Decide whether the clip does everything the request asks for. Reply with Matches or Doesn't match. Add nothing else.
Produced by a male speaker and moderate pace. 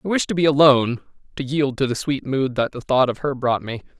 Doesn't match